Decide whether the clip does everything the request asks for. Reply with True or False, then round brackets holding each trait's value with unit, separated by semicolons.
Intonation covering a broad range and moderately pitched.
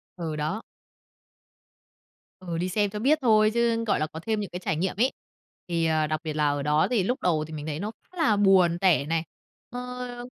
True (5.9 semitones; 180 Hz)